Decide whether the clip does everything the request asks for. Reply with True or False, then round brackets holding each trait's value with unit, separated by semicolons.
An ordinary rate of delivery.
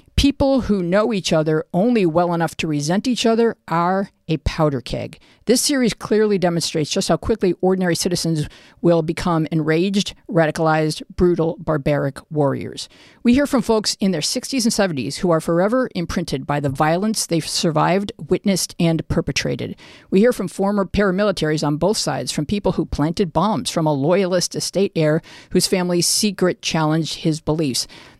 True (165 wpm)